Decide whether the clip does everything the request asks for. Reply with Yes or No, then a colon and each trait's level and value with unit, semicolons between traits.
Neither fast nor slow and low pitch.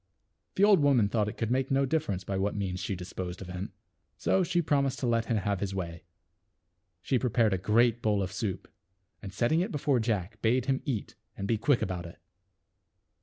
No: fast, 210 wpm; low, 110 Hz